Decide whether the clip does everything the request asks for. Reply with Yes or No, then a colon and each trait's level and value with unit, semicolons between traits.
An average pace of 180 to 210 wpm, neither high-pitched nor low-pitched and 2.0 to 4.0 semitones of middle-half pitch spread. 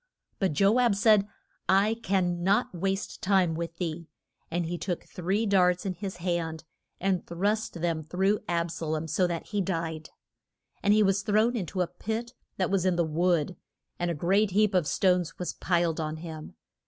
Yes: average, 190 wpm; medium, 180 Hz; average, 2.8 semitones